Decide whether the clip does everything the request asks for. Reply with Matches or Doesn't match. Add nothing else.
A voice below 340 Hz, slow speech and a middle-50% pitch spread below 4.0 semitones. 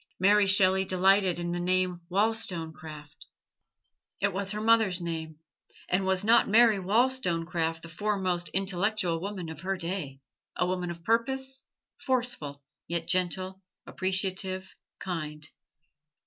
Matches